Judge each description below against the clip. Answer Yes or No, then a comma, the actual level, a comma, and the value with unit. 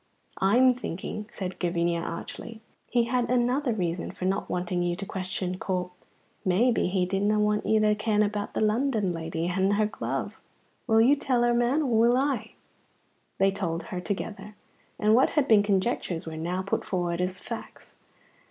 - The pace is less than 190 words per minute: Yes, average, 170 wpm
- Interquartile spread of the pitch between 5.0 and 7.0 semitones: No, average, 4.4 semitones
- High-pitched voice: Yes, high, 205 Hz